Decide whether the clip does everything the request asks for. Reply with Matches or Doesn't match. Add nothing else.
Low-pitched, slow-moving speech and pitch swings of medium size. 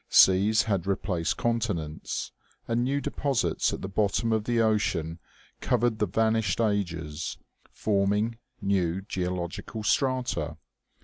Matches